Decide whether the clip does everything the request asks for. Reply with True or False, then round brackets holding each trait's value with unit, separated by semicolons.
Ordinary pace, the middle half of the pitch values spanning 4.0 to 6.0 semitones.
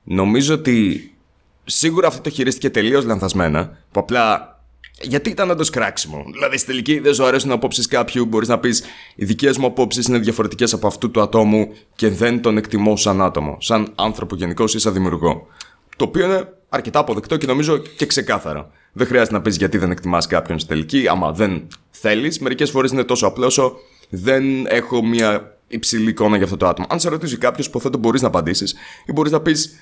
False (190 wpm; 4.7 semitones)